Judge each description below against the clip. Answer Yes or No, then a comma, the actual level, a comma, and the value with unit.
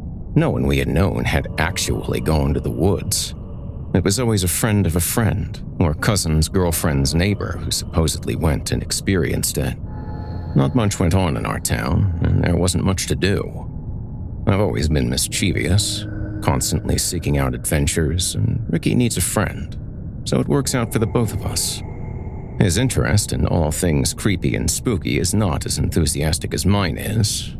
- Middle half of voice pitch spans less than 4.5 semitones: No, average, 5.0 semitones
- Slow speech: No, average, 175 wpm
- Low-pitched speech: Yes, very low, 95 Hz